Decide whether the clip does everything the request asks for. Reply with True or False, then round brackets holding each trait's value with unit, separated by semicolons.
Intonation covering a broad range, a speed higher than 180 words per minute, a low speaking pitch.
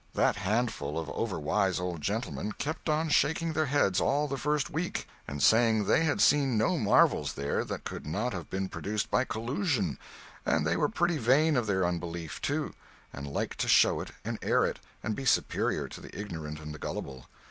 True (9.0 semitones; 195 wpm; 110 Hz)